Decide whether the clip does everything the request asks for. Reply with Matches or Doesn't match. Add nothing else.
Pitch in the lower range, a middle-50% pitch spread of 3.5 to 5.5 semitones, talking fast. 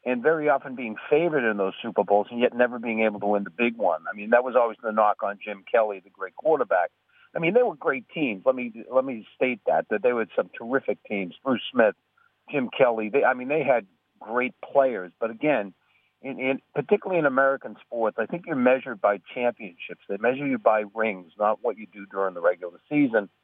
Matches